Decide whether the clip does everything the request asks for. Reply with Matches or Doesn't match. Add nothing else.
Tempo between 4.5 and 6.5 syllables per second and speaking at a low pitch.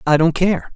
Doesn't match